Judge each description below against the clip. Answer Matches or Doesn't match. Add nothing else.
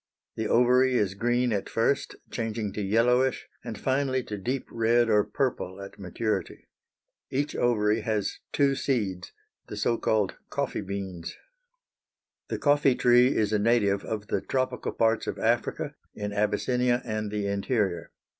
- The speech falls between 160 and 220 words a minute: Doesn't match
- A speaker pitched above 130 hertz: Doesn't match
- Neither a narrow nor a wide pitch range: Matches